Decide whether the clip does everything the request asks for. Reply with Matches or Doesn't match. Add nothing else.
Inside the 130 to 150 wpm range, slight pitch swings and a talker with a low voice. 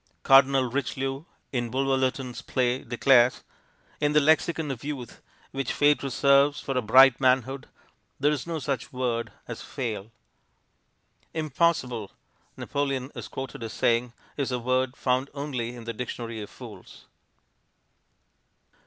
Matches